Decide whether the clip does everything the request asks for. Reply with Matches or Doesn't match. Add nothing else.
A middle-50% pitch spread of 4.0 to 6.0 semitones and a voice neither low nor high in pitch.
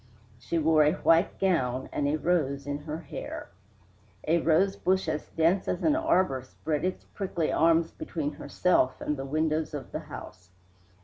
Doesn't match